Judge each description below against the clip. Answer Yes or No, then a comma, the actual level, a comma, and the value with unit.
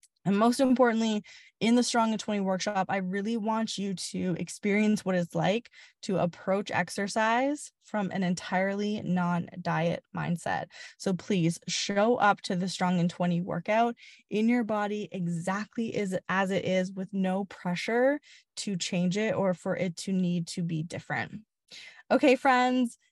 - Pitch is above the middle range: Yes, high, 195 Hz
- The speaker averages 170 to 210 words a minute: No, average, 155 wpm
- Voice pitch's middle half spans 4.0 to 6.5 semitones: No, average, 3.6 semitones